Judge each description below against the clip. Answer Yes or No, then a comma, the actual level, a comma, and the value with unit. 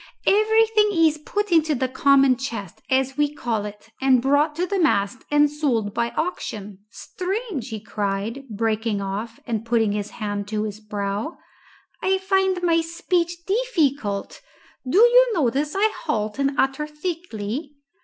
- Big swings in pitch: Yes, wide, 8.0 semitones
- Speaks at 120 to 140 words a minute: No, average, 150 wpm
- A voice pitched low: No, very high, 275 Hz